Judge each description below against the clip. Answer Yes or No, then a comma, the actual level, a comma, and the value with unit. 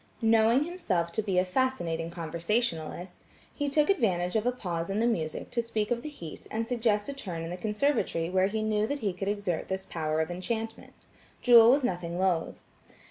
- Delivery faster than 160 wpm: Yes, average, 195 wpm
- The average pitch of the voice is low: No, high, 205 Hz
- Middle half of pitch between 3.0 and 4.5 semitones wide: No, average, 5.3 semitones